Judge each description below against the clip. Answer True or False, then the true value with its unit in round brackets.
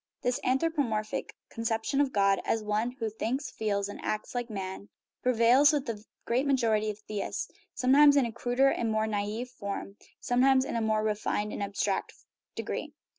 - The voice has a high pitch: True (225 Hz)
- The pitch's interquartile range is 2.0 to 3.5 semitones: True (3.2 semitones)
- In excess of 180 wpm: False (170 wpm)